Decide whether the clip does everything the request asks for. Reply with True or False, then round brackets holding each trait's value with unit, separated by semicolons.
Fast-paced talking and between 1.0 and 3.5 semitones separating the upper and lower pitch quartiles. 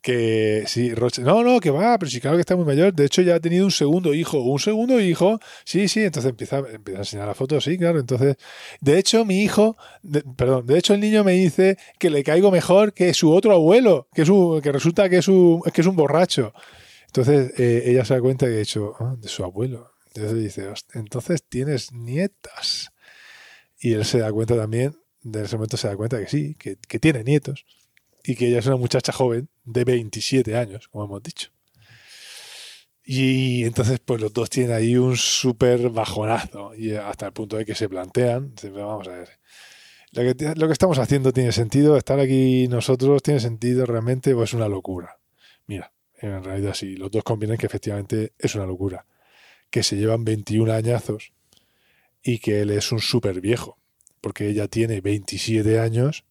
False (200 wpm; 5.4 semitones)